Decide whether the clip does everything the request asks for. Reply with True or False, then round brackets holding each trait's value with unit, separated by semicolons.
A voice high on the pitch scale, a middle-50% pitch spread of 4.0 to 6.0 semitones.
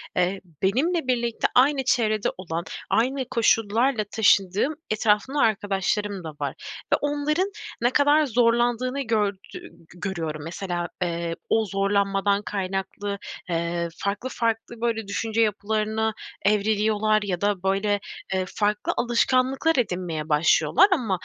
False (210 Hz; 3.6 semitones)